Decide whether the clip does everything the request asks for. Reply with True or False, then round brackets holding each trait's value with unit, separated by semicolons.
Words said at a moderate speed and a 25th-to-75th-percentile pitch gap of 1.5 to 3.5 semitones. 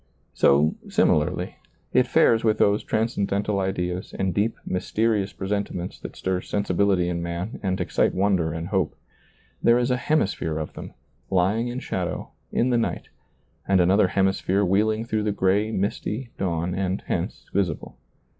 True (150 wpm; 3.0 semitones)